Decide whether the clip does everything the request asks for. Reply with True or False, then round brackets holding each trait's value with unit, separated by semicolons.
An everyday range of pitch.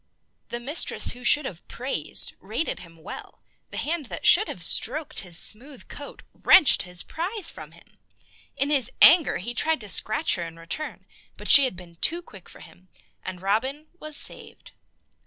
False (8.7 semitones)